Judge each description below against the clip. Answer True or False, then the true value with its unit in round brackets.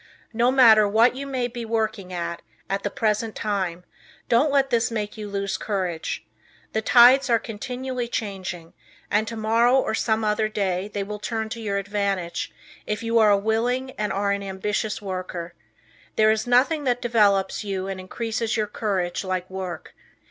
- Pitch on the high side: True (215 Hz)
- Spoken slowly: False (170 wpm)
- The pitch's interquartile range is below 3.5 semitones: True (2.9 semitones)